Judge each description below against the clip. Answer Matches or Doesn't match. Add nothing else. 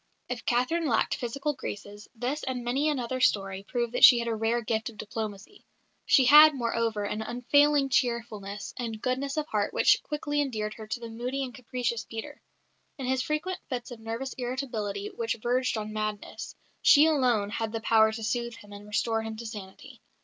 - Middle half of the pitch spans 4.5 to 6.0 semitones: Doesn't match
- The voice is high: Matches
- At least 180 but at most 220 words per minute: Matches